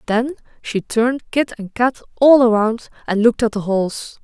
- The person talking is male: No, female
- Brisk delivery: No, average, 185 wpm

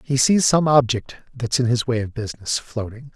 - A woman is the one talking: No, male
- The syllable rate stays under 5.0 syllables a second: No, 5.1 syllables/s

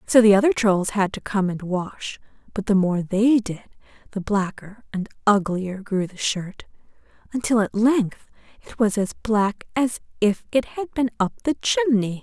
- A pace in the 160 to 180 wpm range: Yes, average, 175 wpm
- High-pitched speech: Yes, high, 210 Hz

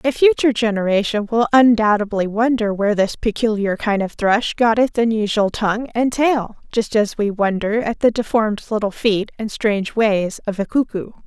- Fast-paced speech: No, average, 175 wpm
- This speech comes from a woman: Yes, female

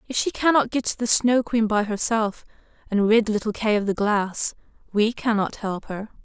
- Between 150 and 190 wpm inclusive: No, average, 200 wpm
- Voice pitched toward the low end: No, high, 220 Hz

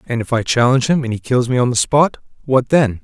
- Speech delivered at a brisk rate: Yes, fast, 275 wpm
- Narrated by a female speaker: No, male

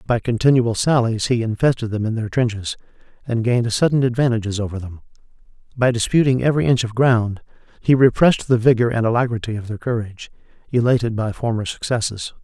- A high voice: No, low, 115 Hz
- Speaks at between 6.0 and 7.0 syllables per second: Yes, 6.2 syllables/s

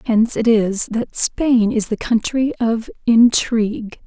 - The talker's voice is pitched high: Yes, high, 225 Hz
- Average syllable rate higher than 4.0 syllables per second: No, 3.8 syllables/s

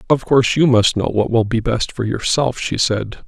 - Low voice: Yes, low, 120 Hz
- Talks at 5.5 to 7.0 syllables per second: No, 4.9 syllables/s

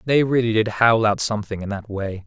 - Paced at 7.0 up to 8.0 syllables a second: No, 5.6 syllables/s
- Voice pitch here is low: Yes, low, 110 Hz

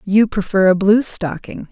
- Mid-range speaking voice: No, high, 200 Hz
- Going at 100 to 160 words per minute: Yes, average, 140 wpm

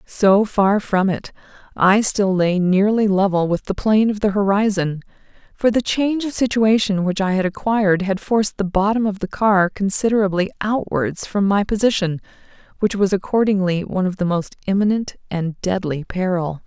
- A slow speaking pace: No, average, 170 wpm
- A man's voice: No, female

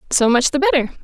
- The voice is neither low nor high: No, very high, 260 Hz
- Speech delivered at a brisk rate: Yes, fast, 230 wpm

